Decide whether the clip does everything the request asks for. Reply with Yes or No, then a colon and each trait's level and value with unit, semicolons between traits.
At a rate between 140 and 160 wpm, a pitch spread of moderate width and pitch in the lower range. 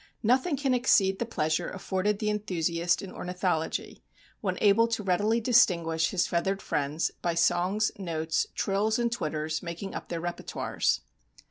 No: average, 145 wpm; average, 4.2 semitones; high, 190 Hz